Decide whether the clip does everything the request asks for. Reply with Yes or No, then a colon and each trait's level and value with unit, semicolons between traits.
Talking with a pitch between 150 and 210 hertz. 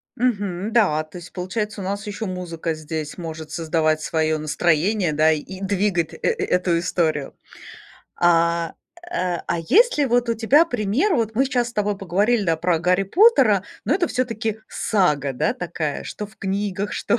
Yes: high, 190 Hz